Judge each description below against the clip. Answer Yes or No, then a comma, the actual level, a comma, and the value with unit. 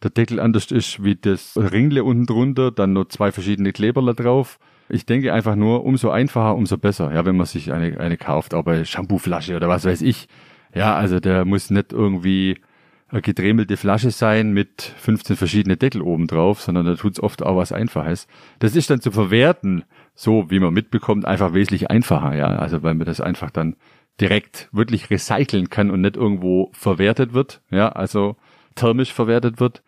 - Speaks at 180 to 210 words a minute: Yes, fast, 190 wpm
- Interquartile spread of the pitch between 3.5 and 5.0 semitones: Yes, average, 4.0 semitones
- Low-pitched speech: Yes, low, 105 Hz